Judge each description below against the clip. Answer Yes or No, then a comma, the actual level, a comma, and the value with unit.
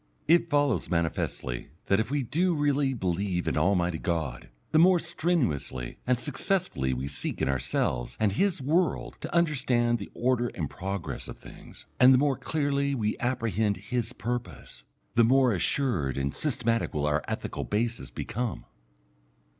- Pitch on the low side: Yes, low, 120 Hz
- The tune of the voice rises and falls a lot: Yes, wide, 8.3 semitones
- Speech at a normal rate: Yes, average, 155 wpm